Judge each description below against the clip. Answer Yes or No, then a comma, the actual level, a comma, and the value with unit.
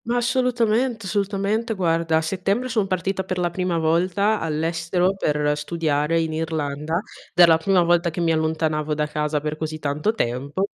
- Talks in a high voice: No, medium, 170 Hz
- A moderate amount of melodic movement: Yes, average, 3.8 semitones